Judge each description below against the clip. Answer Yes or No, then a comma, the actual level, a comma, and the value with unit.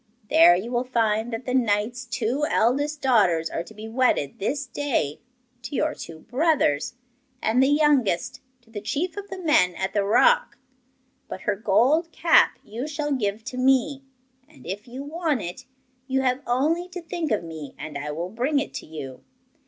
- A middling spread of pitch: No, wide, 6.3 semitones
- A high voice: Yes, very high, 250 Hz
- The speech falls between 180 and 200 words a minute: Yes, average, 185 wpm